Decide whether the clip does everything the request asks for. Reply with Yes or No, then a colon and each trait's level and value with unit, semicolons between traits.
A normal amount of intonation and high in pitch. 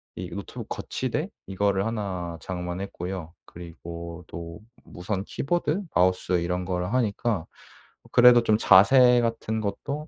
No: average, 4.5 semitones; very low, 95 Hz